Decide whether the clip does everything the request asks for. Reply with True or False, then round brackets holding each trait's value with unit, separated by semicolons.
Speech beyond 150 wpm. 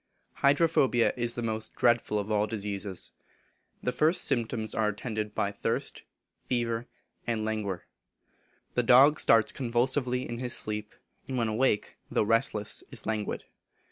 False (140 wpm)